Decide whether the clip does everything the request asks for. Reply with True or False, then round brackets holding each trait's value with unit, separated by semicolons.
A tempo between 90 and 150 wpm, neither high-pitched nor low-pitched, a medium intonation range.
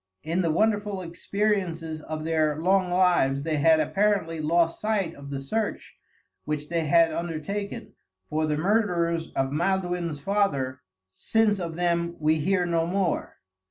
True (145 wpm; 170 Hz; 3.7 semitones)